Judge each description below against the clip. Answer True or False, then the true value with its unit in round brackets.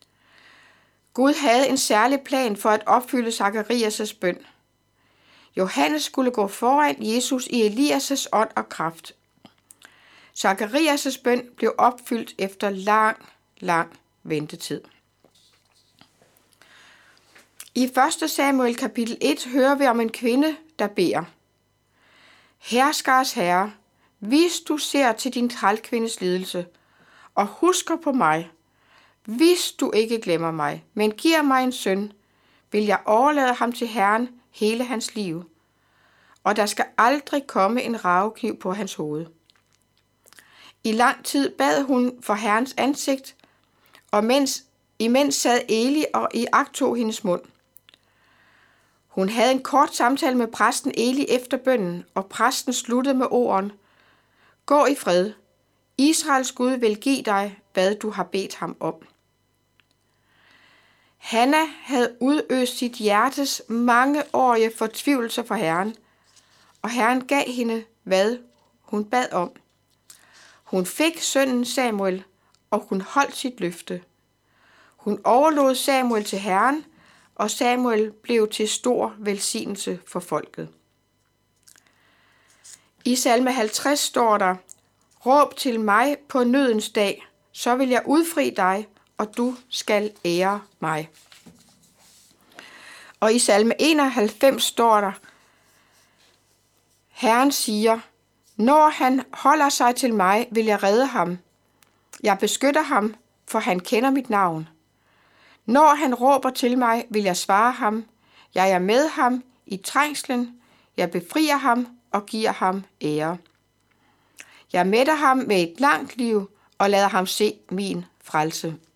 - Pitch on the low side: False (230 Hz)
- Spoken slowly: True (125 wpm)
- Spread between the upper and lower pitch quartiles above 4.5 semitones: True (5.0 semitones)